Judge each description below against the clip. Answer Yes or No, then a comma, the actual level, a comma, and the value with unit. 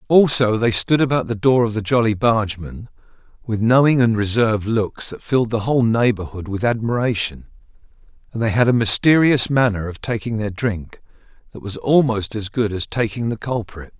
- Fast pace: No, average, 175 wpm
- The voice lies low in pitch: Yes, low, 110 Hz